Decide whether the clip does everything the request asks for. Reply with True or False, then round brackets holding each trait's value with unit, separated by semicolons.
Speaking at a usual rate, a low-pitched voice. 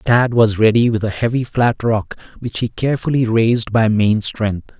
True (190 wpm; 115 Hz)